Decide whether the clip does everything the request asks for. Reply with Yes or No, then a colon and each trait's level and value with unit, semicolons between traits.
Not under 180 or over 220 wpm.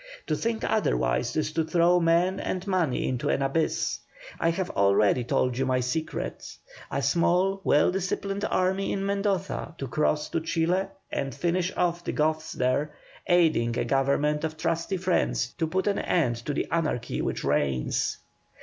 No: average, 165 wpm